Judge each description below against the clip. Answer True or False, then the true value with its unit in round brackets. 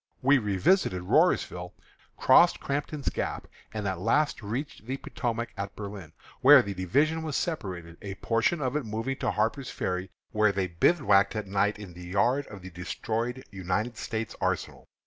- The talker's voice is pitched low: True (105 Hz)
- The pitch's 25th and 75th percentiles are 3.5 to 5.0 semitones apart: False (5.5 semitones)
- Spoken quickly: False (165 wpm)